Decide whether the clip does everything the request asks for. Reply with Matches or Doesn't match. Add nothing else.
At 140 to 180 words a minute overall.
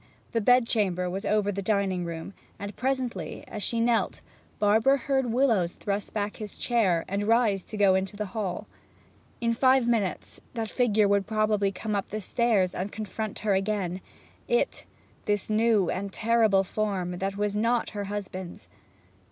Matches